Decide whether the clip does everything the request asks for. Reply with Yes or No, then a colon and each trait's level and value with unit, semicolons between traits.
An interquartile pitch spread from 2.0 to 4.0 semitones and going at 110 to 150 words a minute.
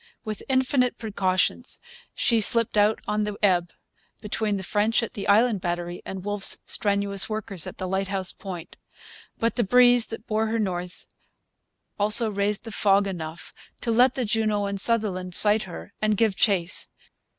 No: average, 2.7 semitones; average, 160 wpm